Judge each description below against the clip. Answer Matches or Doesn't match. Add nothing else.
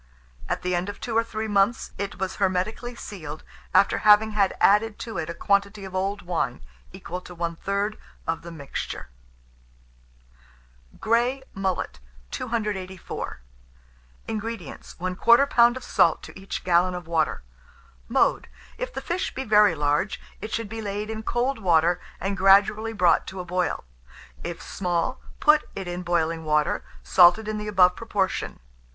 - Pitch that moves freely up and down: Doesn't match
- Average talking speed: Matches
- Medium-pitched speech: Doesn't match